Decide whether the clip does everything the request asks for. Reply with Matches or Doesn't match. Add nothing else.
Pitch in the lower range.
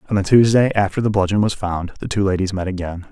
Matches